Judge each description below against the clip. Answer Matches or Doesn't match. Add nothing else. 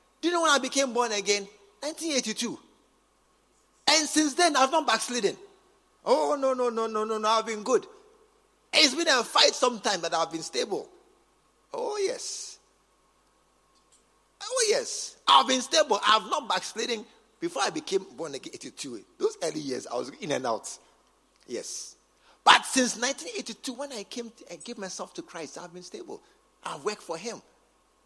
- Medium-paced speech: Matches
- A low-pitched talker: Doesn't match